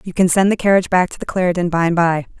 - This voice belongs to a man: No, female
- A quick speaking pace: Yes, fast, 300 wpm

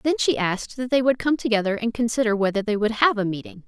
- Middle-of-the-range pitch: No, high, 225 Hz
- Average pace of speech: No, fast, 260 wpm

